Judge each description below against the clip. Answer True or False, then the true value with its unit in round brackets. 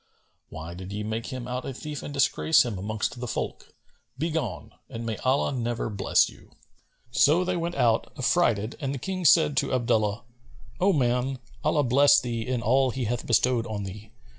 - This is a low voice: True (125 Hz)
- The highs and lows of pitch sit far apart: False (4.2 semitones)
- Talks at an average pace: True (185 wpm)